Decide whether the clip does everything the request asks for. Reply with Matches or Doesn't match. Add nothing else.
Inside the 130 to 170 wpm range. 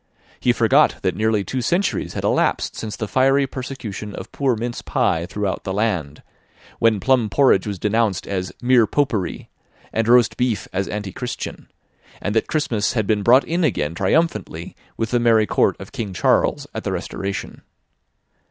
Matches